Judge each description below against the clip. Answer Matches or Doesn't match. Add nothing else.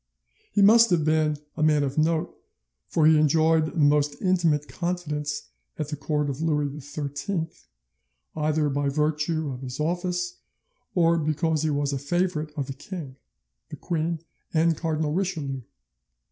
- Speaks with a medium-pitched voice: Matches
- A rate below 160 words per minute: Matches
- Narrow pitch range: Matches